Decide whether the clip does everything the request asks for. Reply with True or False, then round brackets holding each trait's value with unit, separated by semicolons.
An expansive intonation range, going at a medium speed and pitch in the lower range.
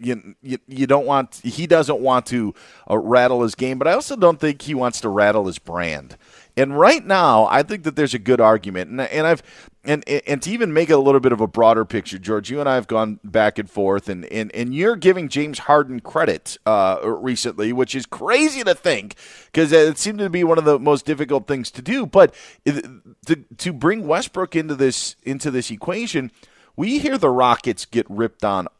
False (5.9 semitones; 215 wpm; 130 Hz)